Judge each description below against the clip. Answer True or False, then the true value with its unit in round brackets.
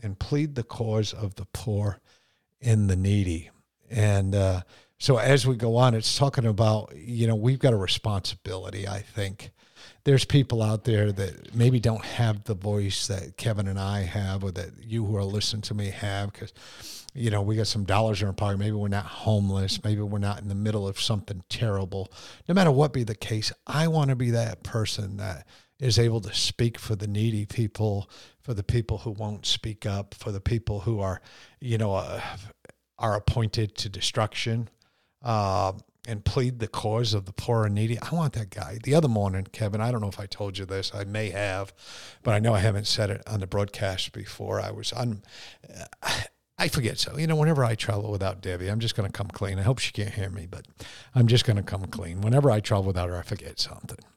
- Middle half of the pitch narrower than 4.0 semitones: True (2.6 semitones)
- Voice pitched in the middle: False (105 Hz)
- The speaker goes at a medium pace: False (215 wpm)